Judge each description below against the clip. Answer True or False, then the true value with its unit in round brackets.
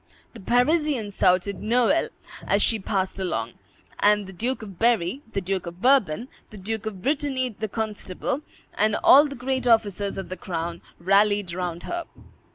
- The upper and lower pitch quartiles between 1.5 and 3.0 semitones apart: False (4.7 semitones)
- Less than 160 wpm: False (165 wpm)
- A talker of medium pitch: False (210 Hz)